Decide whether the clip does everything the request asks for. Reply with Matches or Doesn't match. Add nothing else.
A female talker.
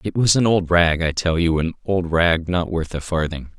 Doesn't match